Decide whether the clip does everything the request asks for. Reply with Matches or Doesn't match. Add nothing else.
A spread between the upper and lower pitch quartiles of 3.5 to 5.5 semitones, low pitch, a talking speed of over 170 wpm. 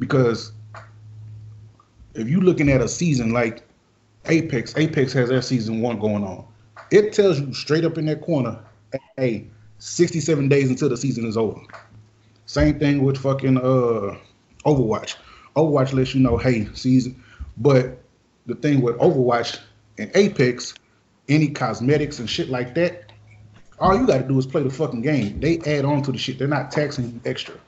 Doesn't match